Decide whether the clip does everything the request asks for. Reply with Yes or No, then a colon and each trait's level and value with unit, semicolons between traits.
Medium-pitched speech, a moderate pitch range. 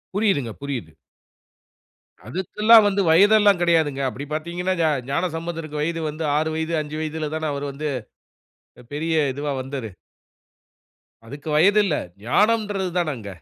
Yes: medium, 160 Hz; average, 4.2 semitones